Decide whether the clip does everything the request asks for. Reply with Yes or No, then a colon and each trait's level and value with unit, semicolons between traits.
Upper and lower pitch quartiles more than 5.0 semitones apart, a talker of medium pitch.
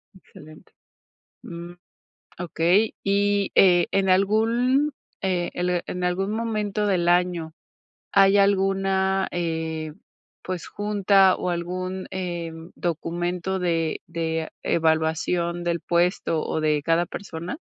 No: narrow, 2.5 semitones; medium, 180 Hz